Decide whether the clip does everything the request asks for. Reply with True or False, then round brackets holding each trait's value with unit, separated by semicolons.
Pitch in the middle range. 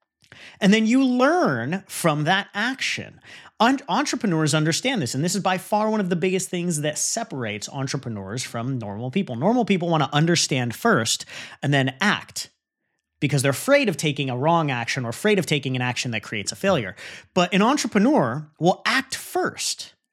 True (170 Hz)